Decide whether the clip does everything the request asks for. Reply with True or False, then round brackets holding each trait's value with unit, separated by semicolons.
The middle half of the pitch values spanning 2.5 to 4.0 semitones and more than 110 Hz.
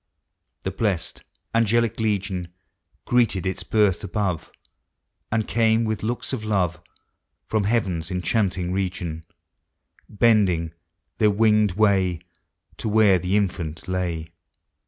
False (3.3 semitones; 100 Hz)